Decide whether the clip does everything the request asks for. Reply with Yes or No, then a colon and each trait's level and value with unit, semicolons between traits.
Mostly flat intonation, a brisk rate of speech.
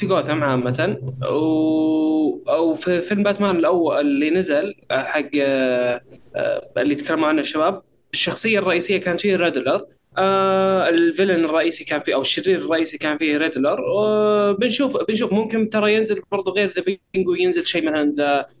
No: average, 4.8 semitones; fast, 145 wpm